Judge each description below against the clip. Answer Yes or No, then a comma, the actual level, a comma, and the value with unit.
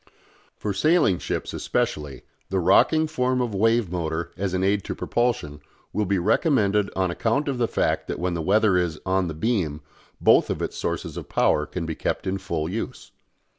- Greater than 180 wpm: Yes, average, 190 wpm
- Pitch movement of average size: Yes, average, 4.9 semitones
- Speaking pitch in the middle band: No, very low, 95 Hz